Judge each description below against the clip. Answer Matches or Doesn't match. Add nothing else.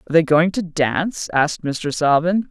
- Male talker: Doesn't match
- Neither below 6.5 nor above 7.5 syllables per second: Doesn't match